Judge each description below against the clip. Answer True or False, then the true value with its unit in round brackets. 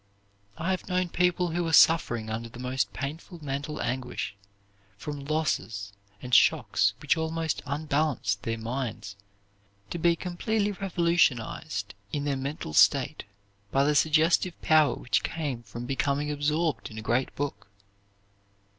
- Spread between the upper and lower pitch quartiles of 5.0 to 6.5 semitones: True (5.3 semitones)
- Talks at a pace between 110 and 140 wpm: True (135 wpm)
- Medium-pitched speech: True (145 Hz)